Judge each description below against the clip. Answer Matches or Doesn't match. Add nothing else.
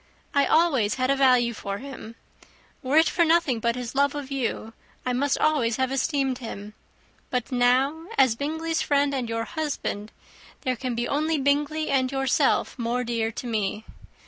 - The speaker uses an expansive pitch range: Doesn't match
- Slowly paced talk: Doesn't match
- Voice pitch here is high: Matches